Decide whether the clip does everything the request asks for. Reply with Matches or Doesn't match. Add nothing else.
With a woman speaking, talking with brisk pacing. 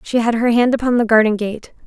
Matches